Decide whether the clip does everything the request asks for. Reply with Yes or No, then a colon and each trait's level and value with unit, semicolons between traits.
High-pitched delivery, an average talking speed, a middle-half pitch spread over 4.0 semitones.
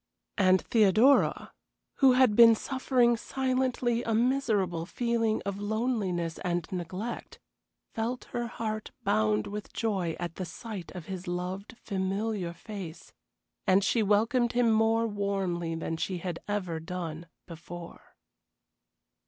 No: high, 205 Hz; slow, 125 wpm; average, 4.6 semitones